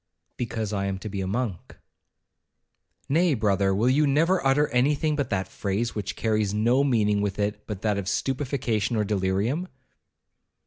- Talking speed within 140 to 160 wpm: No, average, 170 wpm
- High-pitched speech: No, low, 110 Hz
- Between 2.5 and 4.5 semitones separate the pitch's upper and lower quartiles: No, average, 5.1 semitones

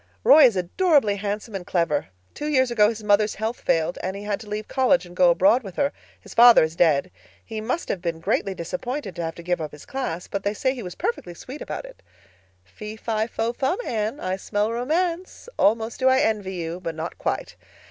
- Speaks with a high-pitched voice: Yes, high, 210 Hz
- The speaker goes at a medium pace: No, fast, 210 wpm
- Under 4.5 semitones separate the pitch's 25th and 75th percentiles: No, wide, 5.5 semitones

